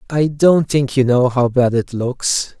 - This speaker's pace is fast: Yes, fast, 210 wpm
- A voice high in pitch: No, low, 130 Hz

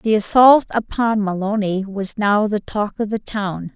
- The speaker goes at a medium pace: Yes, average, 175 wpm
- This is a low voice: No, high, 205 Hz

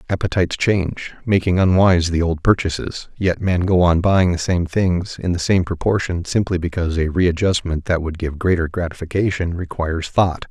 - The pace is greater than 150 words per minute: Yes, average, 170 wpm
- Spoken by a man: Yes, male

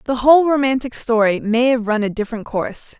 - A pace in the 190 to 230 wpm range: Yes, average, 200 wpm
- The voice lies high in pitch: Yes, high, 240 Hz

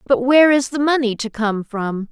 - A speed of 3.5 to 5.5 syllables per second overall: Yes, 5.1 syllables/s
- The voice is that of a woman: Yes, female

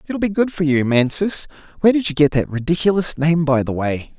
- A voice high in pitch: No, medium, 160 Hz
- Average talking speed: No, fast, 230 wpm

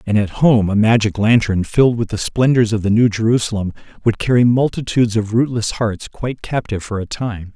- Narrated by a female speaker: No, male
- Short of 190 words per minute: No, average, 200 wpm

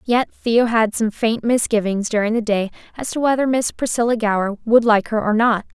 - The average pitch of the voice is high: Yes, high, 225 Hz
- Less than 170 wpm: No, fast, 205 wpm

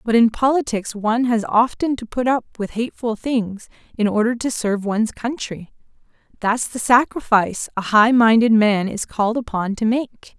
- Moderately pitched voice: No, high, 230 Hz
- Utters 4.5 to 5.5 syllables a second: Yes, 5.0 syllables/s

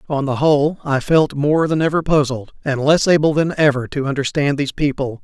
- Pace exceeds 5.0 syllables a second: Yes, 5.6 syllables/s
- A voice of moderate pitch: Yes, medium, 145 Hz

